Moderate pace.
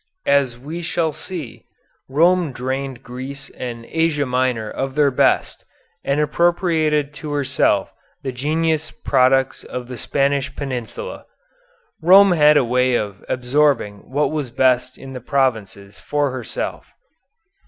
No: slow, 130 wpm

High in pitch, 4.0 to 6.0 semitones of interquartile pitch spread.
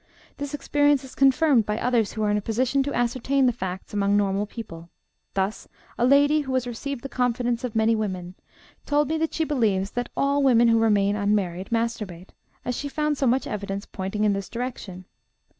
Yes: high, 230 Hz; average, 4.9 semitones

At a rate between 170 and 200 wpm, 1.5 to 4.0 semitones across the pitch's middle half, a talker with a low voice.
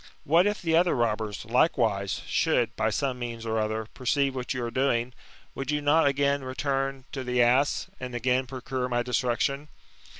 Yes: average, 180 wpm; average, 2.8 semitones; low, 130 Hz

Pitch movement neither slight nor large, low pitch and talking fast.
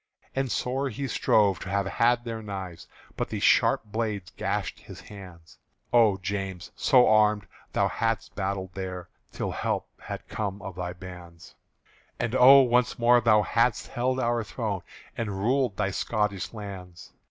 No: average, 3.8 semitones; low, 105 Hz; average, 155 wpm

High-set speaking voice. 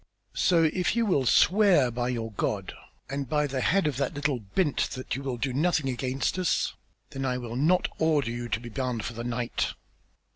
No: low, 135 Hz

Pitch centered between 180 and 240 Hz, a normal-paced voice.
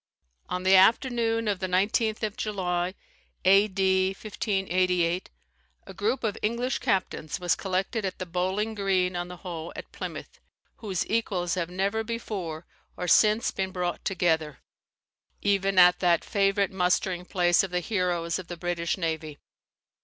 Yes: medium, 185 Hz; average, 145 wpm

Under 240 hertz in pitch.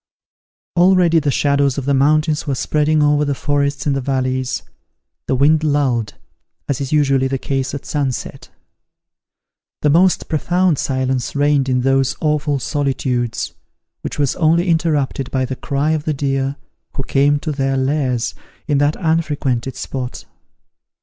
Yes: medium, 140 Hz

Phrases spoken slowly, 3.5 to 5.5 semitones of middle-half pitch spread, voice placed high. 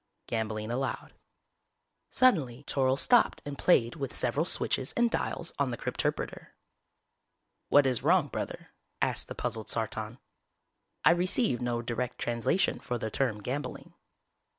No: slow, 130 wpm; average, 3.9 semitones; low, 130 Hz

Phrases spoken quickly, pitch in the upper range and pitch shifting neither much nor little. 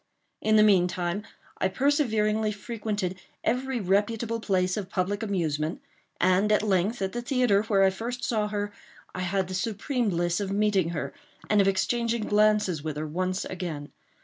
No: average, 165 wpm; high, 200 Hz; average, 3.0 semitones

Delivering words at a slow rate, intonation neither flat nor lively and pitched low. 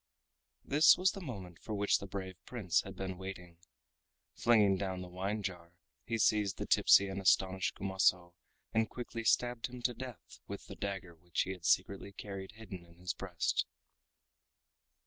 No: average, 165 wpm; average, 3.2 semitones; very low, 95 Hz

